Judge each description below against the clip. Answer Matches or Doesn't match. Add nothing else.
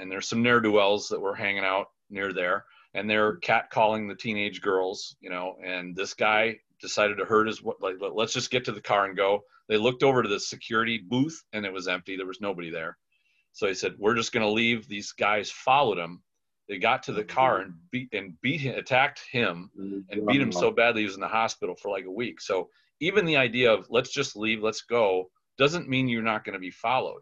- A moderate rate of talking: Doesn't match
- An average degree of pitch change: Matches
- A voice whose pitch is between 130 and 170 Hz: Doesn't match